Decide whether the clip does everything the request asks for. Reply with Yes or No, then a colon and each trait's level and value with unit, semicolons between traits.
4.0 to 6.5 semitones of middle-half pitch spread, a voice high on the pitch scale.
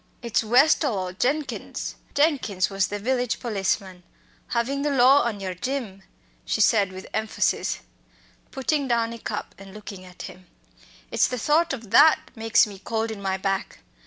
Yes: average, 5.0 semitones; high, 225 Hz